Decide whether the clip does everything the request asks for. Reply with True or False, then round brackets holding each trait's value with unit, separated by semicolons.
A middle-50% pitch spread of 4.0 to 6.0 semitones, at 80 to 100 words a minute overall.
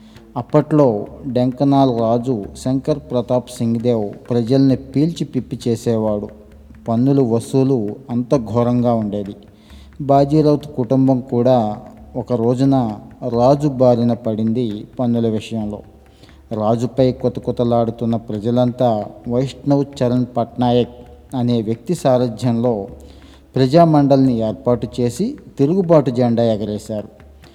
False (3.0 semitones; 90 wpm)